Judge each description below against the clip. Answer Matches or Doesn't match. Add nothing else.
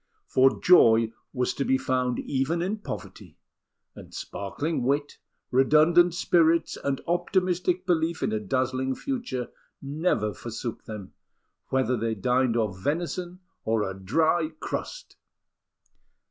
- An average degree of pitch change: Doesn't match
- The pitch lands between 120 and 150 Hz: Matches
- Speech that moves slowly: Matches